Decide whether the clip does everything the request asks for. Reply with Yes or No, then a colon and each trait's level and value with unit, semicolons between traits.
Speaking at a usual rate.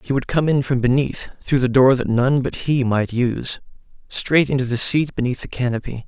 No: fast, 215 wpm